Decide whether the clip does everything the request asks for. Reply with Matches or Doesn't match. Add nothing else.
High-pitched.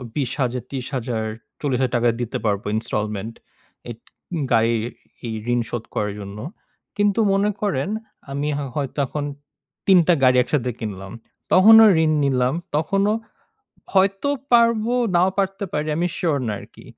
Doesn't match